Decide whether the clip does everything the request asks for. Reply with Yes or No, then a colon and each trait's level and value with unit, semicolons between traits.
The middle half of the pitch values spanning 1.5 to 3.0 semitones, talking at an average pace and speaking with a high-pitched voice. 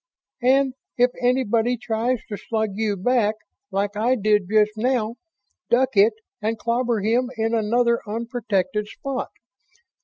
No: narrow, 2.6 semitones; slow, 130 wpm; high, 225 Hz